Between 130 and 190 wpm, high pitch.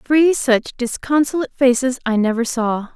Yes: average, 140 wpm; very high, 255 Hz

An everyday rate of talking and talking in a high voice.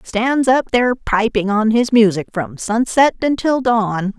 Yes: average, 160 wpm; high, 225 Hz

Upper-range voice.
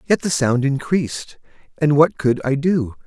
No: medium, 145 Hz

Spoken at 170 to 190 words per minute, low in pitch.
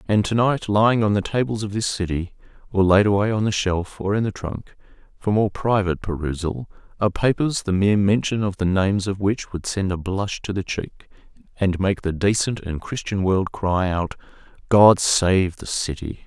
No: average, 200 wpm; low, 100 Hz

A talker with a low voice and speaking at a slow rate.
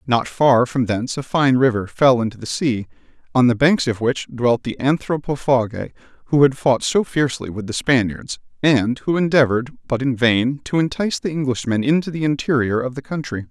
No: low, 130 Hz; average, 190 wpm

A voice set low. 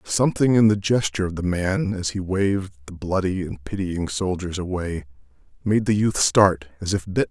Yes: very low, 95 Hz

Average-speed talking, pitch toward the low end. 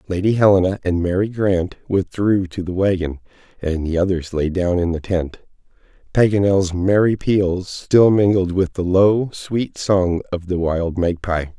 Yes: average, 160 wpm; very low, 95 Hz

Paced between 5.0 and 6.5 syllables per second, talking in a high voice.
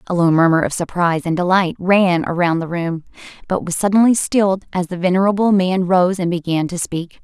No: 5.3 syllables/s; medium, 180 Hz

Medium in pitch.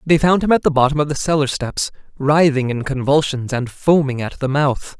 Yes: medium, 145 Hz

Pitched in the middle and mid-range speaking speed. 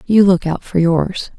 No: medium, 180 Hz; fast, 215 wpm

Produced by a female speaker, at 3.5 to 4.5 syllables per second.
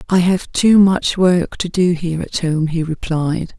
Yes: female; 4.1 syllables/s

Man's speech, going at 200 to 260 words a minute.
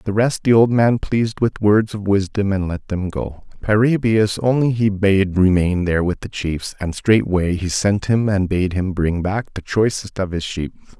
Yes: male; fast, 205 wpm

